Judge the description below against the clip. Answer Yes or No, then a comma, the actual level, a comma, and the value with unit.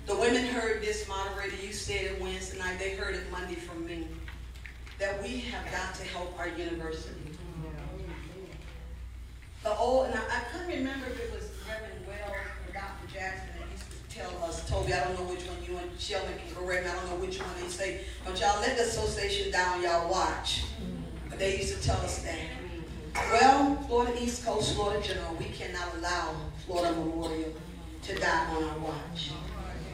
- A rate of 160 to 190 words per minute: Yes, average, 185 wpm